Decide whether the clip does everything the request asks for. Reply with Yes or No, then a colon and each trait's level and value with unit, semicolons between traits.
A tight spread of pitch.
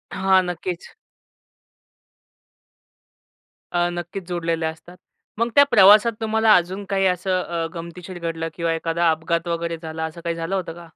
Yes: narrow, 2.2 semitones